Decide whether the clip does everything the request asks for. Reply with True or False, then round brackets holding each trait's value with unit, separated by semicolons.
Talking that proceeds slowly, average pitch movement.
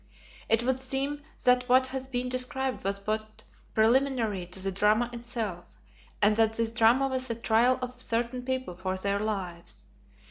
False (165 wpm; 3.3 semitones)